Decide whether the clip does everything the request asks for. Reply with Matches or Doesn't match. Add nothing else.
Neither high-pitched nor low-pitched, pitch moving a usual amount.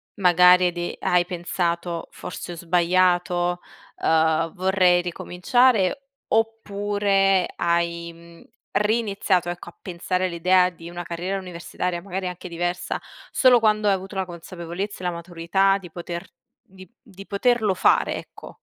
Doesn't match